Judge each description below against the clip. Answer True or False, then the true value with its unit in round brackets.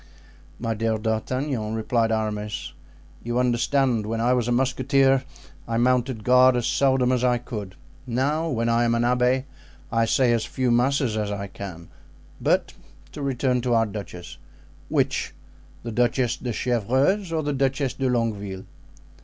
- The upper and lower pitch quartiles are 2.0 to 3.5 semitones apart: True (2.6 semitones)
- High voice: False (120 Hz)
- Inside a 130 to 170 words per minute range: True (155 wpm)